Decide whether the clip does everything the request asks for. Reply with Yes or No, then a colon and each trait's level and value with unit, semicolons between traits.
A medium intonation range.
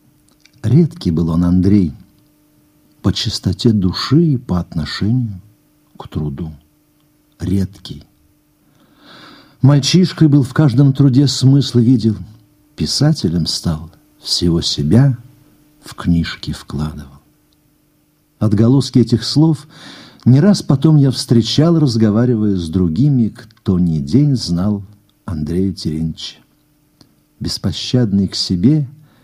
No: wide, 7.9 semitones